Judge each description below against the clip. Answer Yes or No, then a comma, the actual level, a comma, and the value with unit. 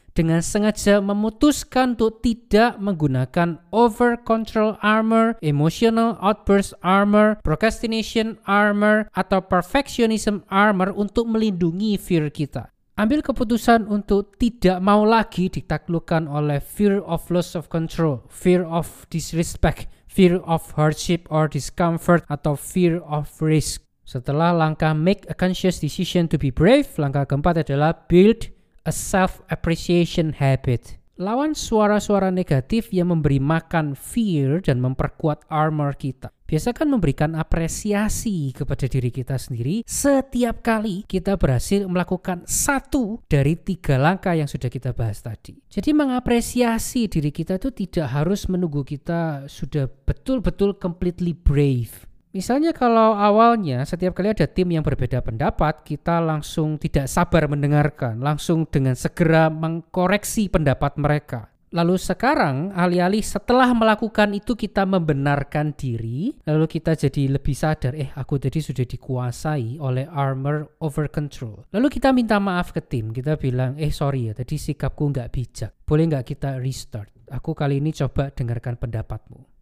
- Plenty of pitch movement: Yes, wide, 6.2 semitones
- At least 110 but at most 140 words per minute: Yes, average, 135 wpm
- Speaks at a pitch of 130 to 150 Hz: No, medium, 165 Hz